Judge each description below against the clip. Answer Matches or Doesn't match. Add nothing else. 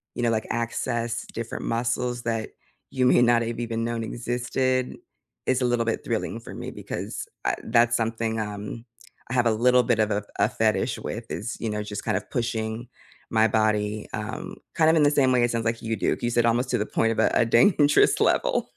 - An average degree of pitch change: Doesn't match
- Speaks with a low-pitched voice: Matches